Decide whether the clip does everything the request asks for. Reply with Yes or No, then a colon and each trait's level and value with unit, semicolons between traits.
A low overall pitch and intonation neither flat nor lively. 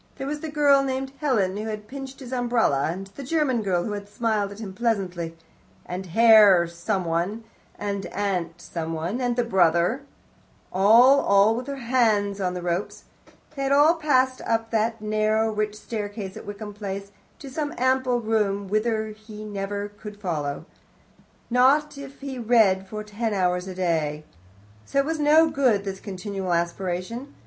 No: high, 215 Hz; average, 4.8 semitones